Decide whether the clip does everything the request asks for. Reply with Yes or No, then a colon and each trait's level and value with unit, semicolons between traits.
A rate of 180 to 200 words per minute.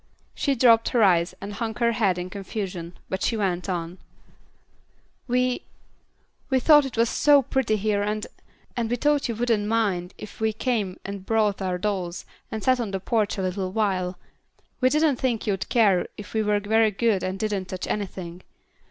Yes: average, 185 wpm